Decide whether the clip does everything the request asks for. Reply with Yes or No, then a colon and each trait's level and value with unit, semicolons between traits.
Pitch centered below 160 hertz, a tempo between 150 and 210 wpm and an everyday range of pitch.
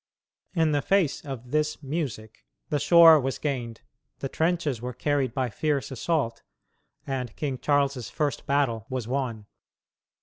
No: medium, 140 Hz; average, 140 wpm; average, 3.4 semitones